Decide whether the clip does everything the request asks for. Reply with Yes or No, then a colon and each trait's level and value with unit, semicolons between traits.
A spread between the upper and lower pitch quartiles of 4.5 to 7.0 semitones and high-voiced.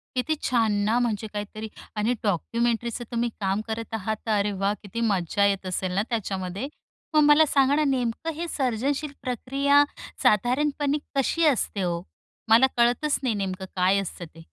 Yes: average, 5.0 semitones; high, 230 Hz